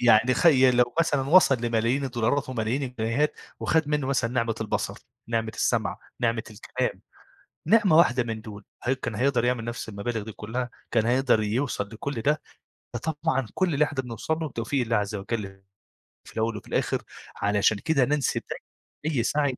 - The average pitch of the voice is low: Yes, low, 120 Hz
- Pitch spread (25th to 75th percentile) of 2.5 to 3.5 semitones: No, average, 3.9 semitones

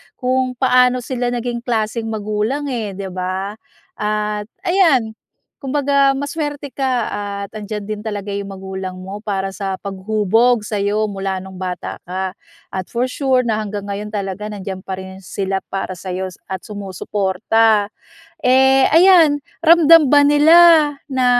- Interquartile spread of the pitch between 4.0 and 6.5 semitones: Yes, average, 5.0 semitones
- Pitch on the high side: Yes, high, 210 Hz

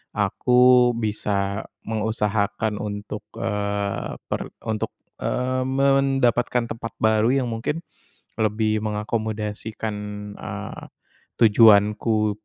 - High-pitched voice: No, low, 110 Hz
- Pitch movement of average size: No, narrow, 2.2 semitones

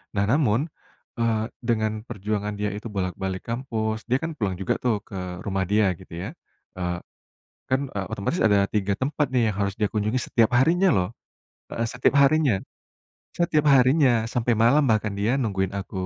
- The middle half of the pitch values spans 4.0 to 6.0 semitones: Yes, average, 4.3 semitones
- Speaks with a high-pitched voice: No, low, 110 Hz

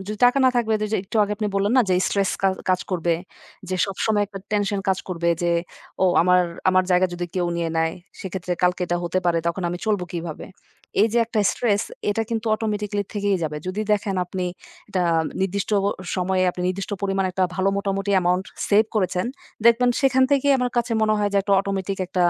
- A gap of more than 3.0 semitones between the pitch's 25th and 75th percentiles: No, narrow, 2.5 semitones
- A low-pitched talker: No, high, 195 Hz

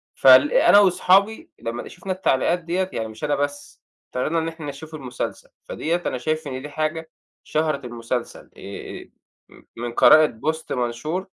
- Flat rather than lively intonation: No, average, 5.1 semitones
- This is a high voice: No, medium, 155 Hz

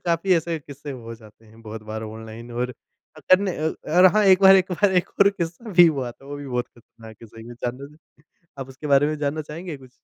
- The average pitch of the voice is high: No, medium, 140 Hz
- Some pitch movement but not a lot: No, wide, 6.3 semitones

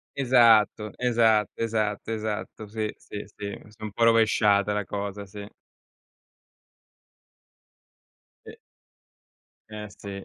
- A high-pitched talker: No, low, 105 Hz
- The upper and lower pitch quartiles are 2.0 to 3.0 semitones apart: No, narrow, 1.6 semitones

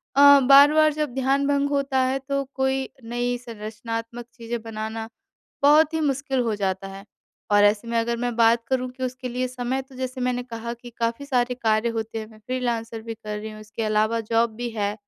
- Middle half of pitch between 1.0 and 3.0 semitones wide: Yes, average, 2.7 semitones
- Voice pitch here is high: Yes, high, 240 Hz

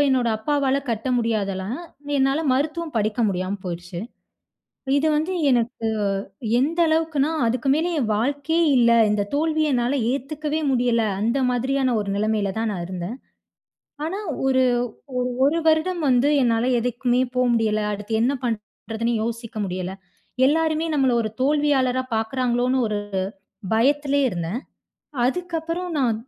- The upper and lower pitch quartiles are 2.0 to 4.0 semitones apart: No, average, 4.7 semitones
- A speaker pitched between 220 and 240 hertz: No, very high, 250 Hz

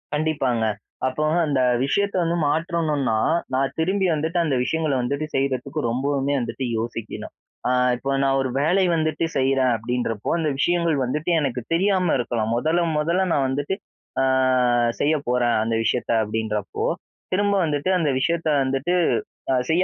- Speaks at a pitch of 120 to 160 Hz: Yes, medium, 140 Hz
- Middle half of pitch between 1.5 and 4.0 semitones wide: No, average, 4.4 semitones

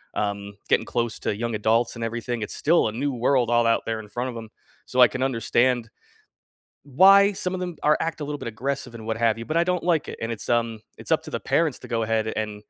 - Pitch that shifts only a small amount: No, average, 3.9 semitones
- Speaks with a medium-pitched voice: No, low, 120 Hz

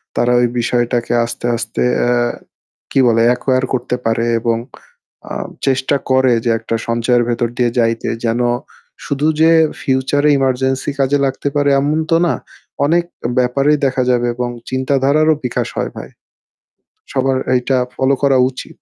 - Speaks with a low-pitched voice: Yes, low, 130 Hz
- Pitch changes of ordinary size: No, narrow, 2.2 semitones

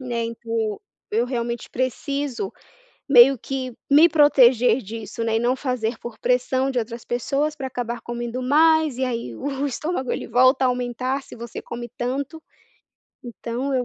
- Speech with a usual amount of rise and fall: No, narrow, 2.3 semitones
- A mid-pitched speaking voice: No, very high, 250 Hz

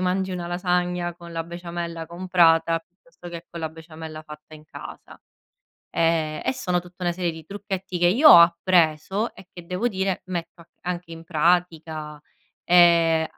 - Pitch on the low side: No, medium, 170 Hz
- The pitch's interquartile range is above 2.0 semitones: No, narrow, 1.7 semitones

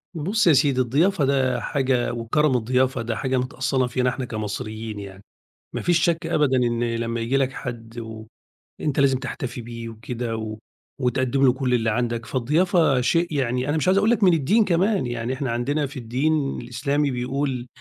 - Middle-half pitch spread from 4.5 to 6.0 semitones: No, average, 3.6 semitones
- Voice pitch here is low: Yes, low, 130 Hz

